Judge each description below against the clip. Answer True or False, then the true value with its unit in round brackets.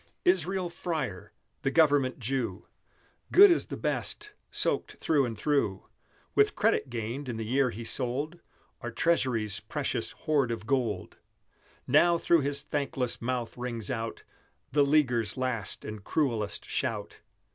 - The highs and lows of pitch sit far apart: False (4.5 semitones)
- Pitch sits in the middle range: False (130 Hz)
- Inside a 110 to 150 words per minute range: True (135 wpm)